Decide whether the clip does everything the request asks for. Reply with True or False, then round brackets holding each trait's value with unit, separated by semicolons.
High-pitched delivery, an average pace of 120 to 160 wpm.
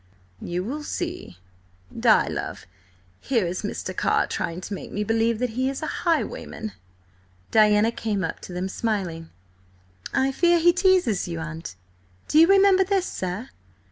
True (225 Hz; 155 wpm)